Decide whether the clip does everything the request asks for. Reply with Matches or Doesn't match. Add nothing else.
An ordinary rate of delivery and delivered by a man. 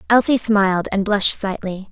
Doesn't match